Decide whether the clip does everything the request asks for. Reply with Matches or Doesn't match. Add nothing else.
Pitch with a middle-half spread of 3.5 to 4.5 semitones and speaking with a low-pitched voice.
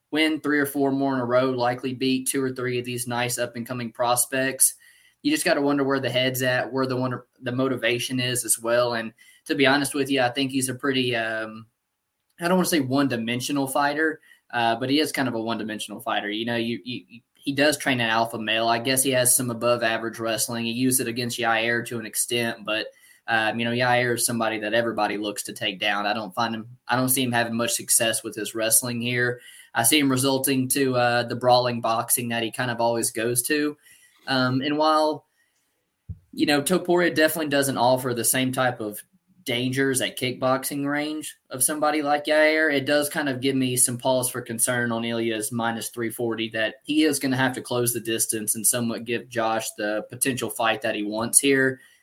Doesn't match